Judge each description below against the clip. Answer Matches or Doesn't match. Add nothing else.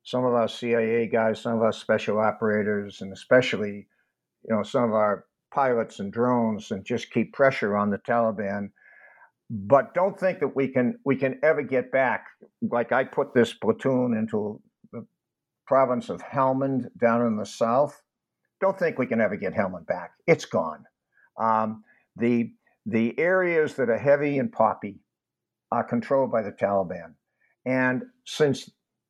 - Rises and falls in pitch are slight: Doesn't match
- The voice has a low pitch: Matches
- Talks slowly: Doesn't match